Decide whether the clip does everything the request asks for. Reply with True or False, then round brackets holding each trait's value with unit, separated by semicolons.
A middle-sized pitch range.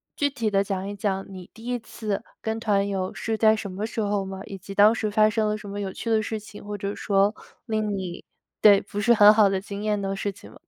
False (1.6 semitones)